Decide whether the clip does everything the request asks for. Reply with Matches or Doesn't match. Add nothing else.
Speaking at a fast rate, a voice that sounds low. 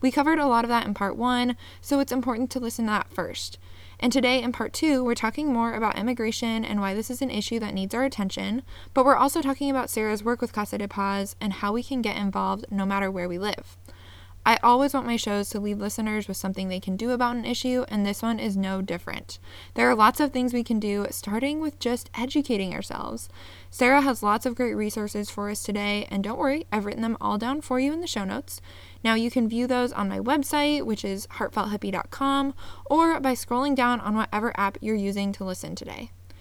Doesn't match